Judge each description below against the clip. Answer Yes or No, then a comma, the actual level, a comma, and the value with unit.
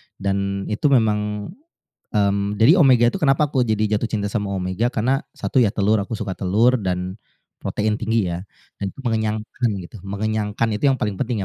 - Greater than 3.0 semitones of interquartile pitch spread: No, average, 2.7 semitones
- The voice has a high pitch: No, low, 105 Hz